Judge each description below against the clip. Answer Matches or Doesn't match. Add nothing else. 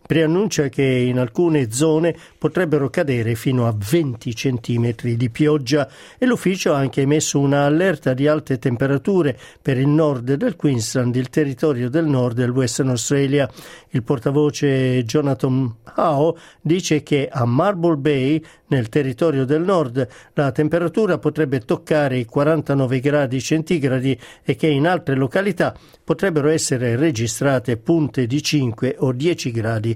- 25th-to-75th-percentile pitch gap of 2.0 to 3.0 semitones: Doesn't match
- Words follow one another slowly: Doesn't match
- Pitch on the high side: Doesn't match